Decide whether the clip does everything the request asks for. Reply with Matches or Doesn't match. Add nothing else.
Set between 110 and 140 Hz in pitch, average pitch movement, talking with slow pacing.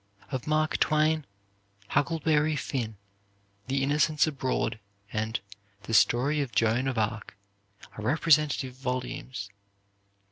Matches